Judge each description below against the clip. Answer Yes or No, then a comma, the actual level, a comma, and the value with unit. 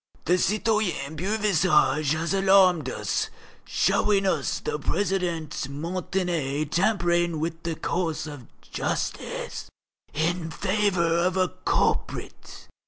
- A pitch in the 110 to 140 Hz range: No, medium, 175 Hz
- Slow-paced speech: Yes, slow, 105 wpm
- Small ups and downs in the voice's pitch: No, average, 3.3 semitones